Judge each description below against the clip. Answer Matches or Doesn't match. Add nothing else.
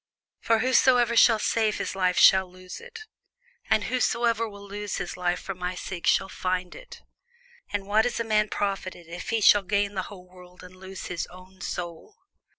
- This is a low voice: Doesn't match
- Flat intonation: Doesn't match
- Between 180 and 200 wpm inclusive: Matches